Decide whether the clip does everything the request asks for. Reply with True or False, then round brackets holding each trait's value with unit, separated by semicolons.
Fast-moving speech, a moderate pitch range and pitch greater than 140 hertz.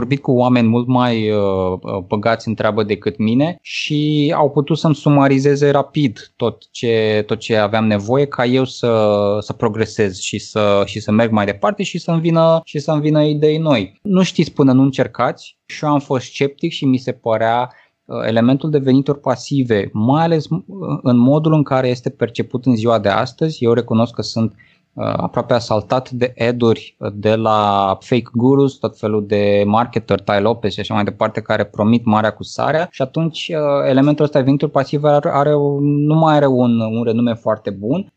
False (180 wpm; 4.7 semitones; 125 Hz)